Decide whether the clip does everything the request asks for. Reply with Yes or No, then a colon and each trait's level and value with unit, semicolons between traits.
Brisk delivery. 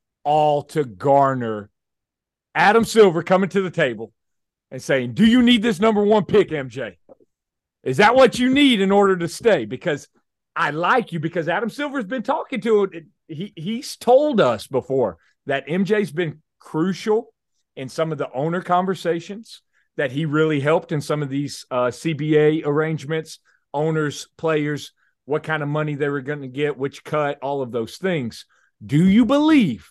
No: average, 175 wpm